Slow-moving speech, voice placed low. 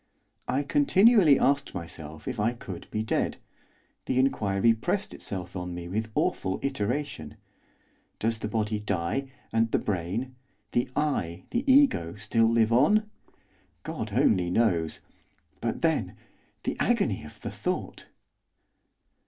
Yes: slow, 130 wpm; low, 110 Hz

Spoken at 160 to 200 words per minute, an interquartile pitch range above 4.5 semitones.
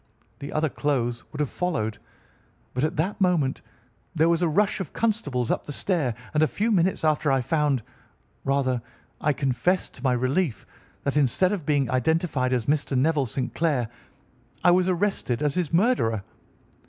Yes: average, 170 wpm; average, 5.3 semitones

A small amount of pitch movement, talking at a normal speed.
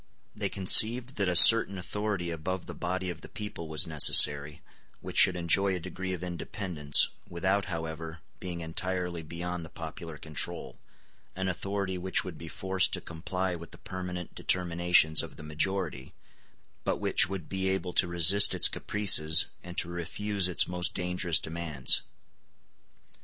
Yes: narrow, 2.3 semitones; average, 155 wpm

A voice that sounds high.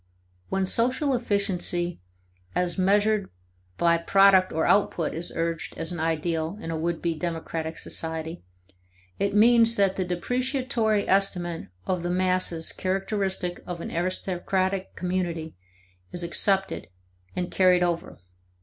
No: medium, 180 Hz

